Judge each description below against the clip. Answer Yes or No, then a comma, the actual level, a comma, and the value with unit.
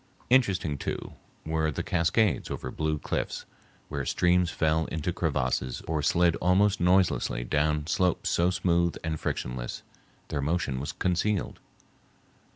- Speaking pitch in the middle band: No, very low, 85 Hz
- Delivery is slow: Yes, slow, 130 wpm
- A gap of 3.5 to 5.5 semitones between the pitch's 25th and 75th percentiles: No, average, 2.9 semitones